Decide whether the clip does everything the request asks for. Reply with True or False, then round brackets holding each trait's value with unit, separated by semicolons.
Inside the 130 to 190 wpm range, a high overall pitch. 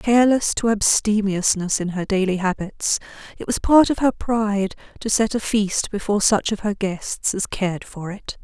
True (185 wpm; 205 Hz)